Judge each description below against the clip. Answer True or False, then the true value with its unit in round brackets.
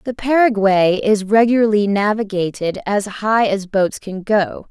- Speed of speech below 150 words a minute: True (140 wpm)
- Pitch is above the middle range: True (205 Hz)